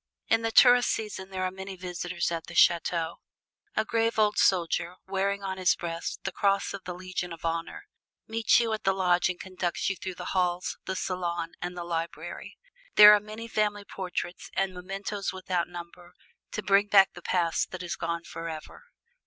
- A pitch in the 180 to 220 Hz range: Yes, medium, 185 Hz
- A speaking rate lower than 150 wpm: No, average, 185 wpm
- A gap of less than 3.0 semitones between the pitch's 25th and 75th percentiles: Yes, narrow, 2.4 semitones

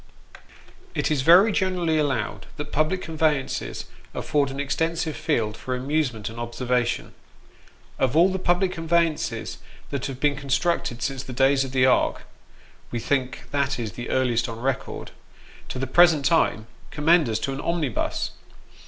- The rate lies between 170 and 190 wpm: No, average, 155 wpm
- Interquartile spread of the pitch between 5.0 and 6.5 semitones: No, average, 4.3 semitones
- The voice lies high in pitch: No, medium, 140 Hz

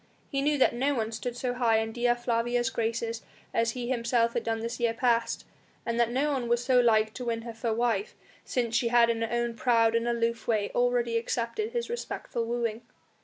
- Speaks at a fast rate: Yes, fast, 215 wpm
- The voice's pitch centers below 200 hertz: No, high, 235 Hz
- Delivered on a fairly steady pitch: Yes, narrow, 1.1 semitones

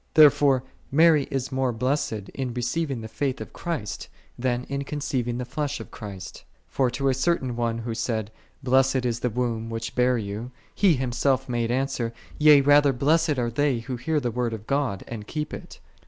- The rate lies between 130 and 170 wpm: No, average, 200 wpm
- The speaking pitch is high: No, low, 125 Hz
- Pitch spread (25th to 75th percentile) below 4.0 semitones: Yes, average, 3.0 semitones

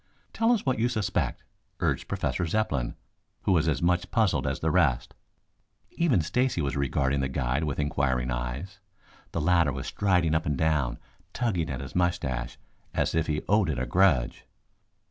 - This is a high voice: No, very low, 80 Hz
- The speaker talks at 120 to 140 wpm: No, average, 170 wpm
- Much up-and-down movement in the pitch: Yes, wide, 5.7 semitones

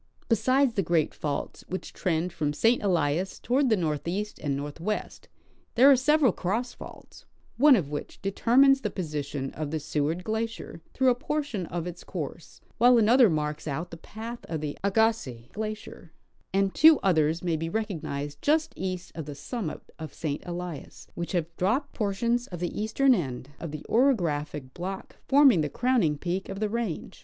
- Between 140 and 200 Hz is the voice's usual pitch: Yes, medium, 185 Hz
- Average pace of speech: Yes, average, 175 wpm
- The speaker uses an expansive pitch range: Yes, wide, 6.8 semitones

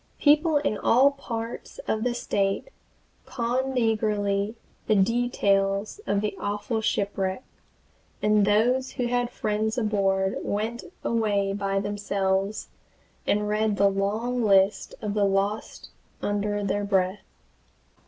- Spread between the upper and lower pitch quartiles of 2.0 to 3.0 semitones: Yes, average, 2.7 semitones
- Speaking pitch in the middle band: No, high, 210 Hz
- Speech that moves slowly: Yes, slow, 120 wpm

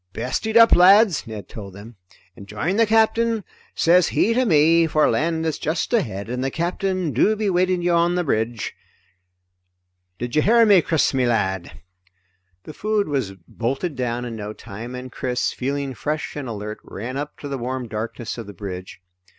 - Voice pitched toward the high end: No, medium, 140 Hz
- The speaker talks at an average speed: Yes, average, 175 wpm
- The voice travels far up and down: Yes, wide, 7.4 semitones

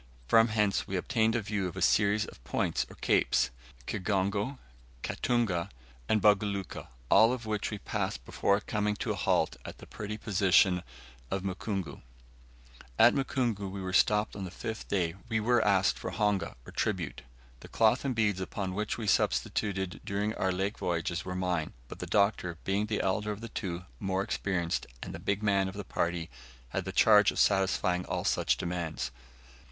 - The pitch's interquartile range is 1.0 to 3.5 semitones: Yes, narrow, 2.4 semitones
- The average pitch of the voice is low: Yes, low, 100 Hz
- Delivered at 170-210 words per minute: Yes, average, 180 wpm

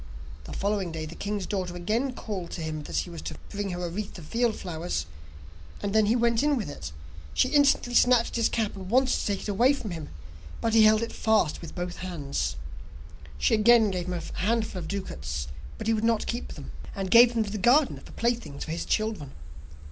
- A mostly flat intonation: No, average, 4.8 semitones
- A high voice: Yes, high, 205 Hz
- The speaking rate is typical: No, fast, 225 wpm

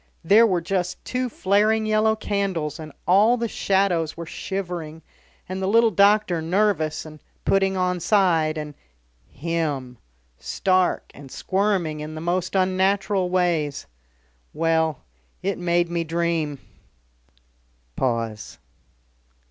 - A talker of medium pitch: Yes, medium, 180 Hz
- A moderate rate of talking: No, slow, 115 wpm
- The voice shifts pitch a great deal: No, average, 3.7 semitones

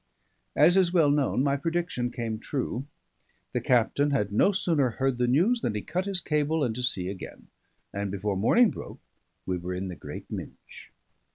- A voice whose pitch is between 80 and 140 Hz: Yes, low, 135 Hz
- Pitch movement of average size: No, wide, 7.3 semitones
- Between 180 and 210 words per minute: Yes, average, 185 wpm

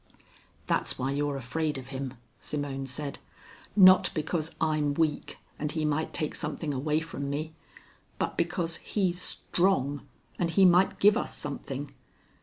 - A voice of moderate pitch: Yes, medium, 150 Hz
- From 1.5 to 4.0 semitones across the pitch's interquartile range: Yes, average, 3.0 semitones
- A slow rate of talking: No, average, 145 wpm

